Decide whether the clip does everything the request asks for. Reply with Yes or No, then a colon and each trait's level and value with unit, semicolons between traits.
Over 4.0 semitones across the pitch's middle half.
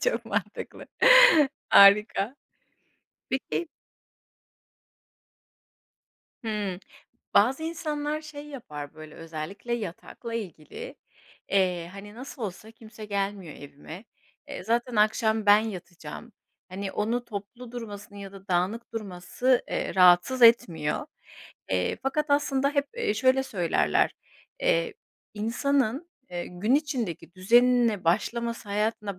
Yes: average, 5.2 semitones